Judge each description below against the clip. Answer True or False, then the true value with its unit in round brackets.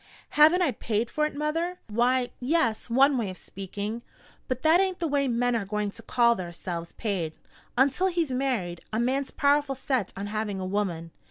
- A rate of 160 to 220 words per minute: True (185 wpm)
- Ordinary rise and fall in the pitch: False (5.7 semitones)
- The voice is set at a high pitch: True (245 Hz)